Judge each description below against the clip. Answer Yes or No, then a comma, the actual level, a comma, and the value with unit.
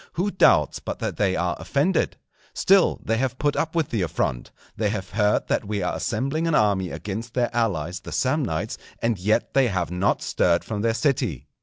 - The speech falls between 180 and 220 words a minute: Yes, average, 195 wpm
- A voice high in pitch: No, low, 110 Hz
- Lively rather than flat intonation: Yes, wide, 6.3 semitones